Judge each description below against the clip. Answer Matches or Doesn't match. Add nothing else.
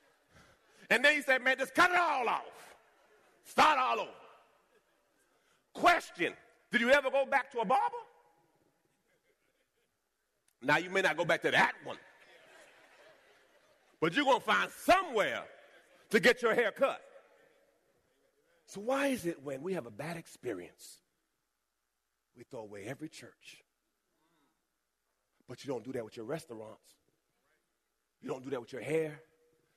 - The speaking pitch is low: Doesn't match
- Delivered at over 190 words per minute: Doesn't match